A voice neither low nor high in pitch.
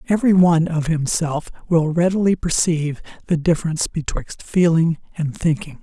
Yes: medium, 165 Hz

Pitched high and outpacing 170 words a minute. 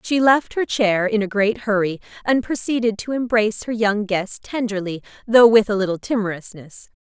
Yes: high, 215 Hz; average, 180 wpm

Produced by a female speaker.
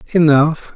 No: male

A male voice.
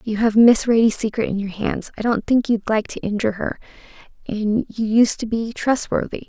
No: female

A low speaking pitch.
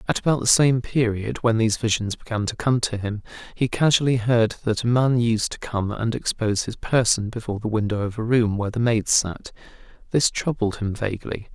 Yes: low, 115 Hz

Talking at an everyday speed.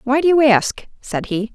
No: fast, 235 wpm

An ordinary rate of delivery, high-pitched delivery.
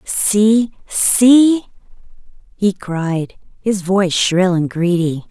No: slow, 100 wpm; high, 195 Hz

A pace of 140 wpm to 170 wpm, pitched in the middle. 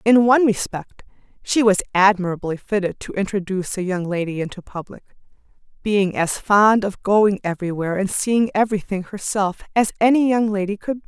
No: average, 165 wpm; high, 200 Hz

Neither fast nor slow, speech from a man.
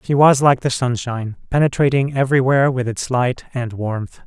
Yes: average, 170 wpm; male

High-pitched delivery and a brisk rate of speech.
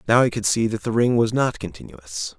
No: low, 110 Hz; fast, 250 wpm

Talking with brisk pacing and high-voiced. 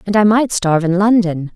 Yes: fast, 230 wpm; high, 195 Hz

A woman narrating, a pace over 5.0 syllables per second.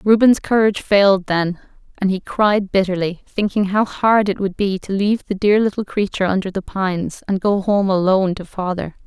Yes: female; 5.4 syllables/s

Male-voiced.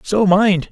Yes: male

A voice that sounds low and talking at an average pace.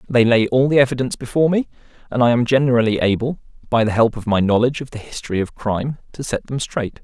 No: low, 120 Hz; fast, 230 wpm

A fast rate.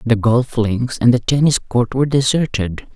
No: average, 185 wpm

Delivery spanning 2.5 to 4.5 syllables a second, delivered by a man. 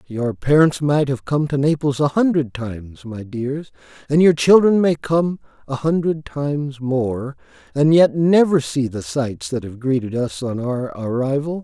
Yes: 4.3 syllables/s; male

